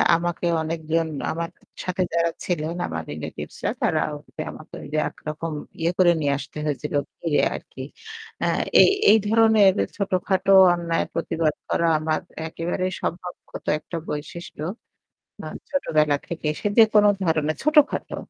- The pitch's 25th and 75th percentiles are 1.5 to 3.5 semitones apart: Yes, average, 3.0 semitones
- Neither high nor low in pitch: Yes, medium, 165 Hz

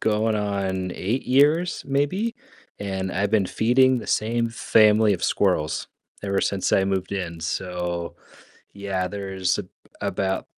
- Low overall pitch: Yes, low, 100 Hz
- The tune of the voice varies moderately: Yes, average, 3.3 semitones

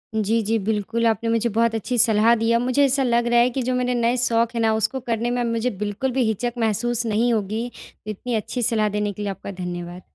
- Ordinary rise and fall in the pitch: No, narrow, 2.0 semitones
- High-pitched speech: Yes, high, 230 Hz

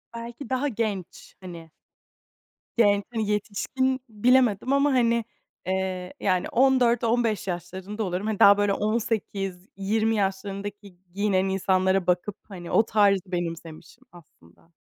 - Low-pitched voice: No, high, 205 Hz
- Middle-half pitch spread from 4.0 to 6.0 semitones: No, average, 3.4 semitones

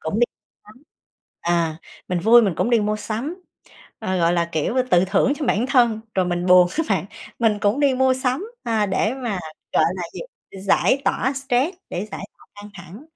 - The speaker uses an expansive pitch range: Yes, wide, 5.8 semitones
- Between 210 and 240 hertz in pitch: Yes, high, 215 Hz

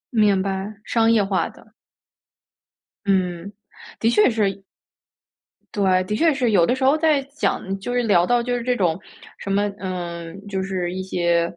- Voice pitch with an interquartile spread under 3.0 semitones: No, average, 4.0 semitones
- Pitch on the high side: Yes, high, 195 Hz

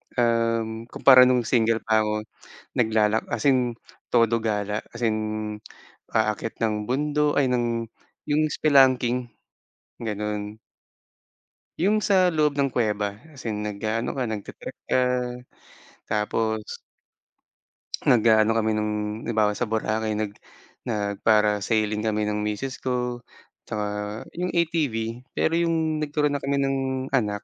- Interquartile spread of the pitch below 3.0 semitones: No, average, 3.4 semitones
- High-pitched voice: No, low, 115 Hz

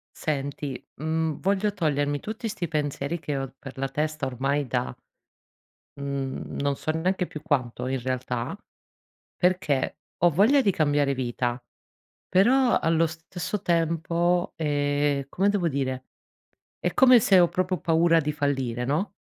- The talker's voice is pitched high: No, medium, 150 Hz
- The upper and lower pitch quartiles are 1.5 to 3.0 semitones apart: No, average, 4.2 semitones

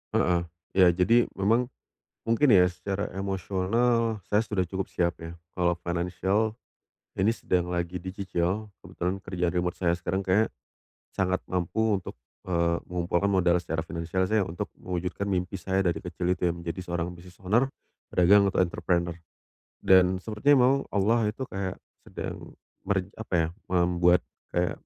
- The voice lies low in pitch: Yes, very low, 90 Hz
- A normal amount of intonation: No, narrow, 2.3 semitones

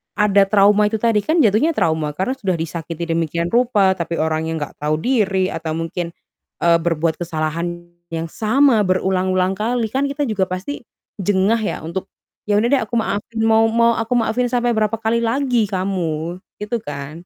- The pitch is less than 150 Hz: No, high, 195 Hz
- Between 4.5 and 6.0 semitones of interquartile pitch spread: Yes, average, 5.0 semitones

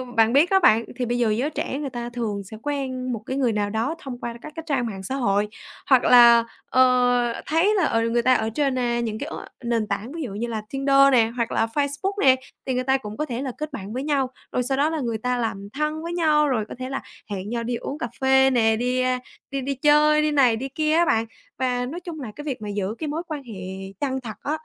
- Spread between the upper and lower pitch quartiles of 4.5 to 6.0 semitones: No, average, 3.8 semitones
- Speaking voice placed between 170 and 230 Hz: No, very high, 255 Hz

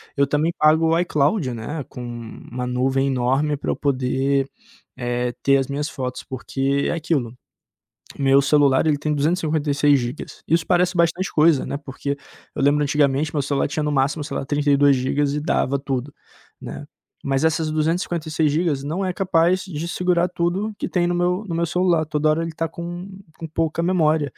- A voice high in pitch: No, medium, 150 Hz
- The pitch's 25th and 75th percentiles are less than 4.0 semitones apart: Yes, average, 3.2 semitones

